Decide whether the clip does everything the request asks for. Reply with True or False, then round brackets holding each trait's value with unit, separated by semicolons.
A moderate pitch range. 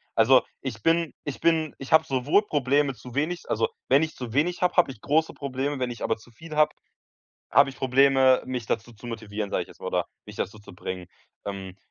True (4.8 semitones)